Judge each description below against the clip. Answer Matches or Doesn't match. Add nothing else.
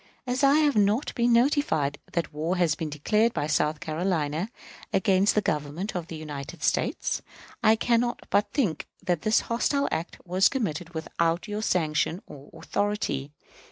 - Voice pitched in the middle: Matches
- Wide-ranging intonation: Matches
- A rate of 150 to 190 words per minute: Matches